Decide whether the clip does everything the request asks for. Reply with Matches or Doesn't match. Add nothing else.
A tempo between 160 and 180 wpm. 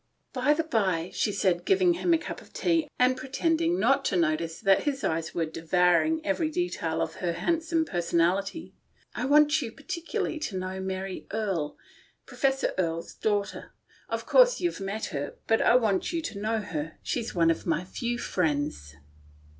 Doesn't match